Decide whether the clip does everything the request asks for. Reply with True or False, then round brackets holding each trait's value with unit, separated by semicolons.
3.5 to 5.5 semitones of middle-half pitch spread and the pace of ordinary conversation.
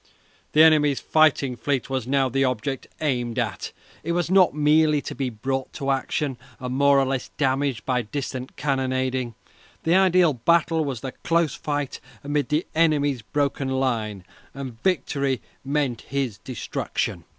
False (2.6 semitones; 150 wpm)